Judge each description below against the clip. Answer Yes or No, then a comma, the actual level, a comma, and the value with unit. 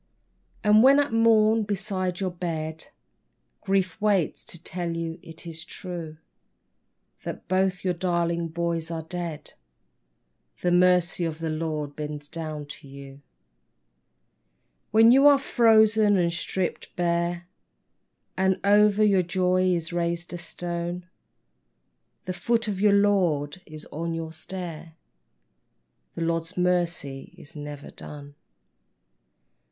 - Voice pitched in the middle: Yes, medium, 175 Hz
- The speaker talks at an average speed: No, slow, 125 wpm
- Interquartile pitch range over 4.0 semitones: No, average, 2.8 semitones